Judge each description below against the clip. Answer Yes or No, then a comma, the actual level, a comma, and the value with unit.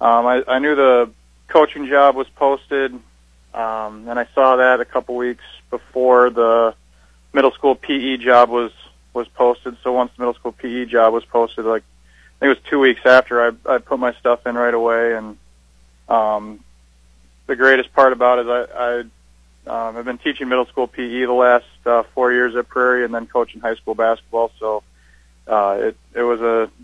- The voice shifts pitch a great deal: No, average, 2.7 semitones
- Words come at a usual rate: Yes, average, 190 wpm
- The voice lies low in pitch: Yes, low, 120 Hz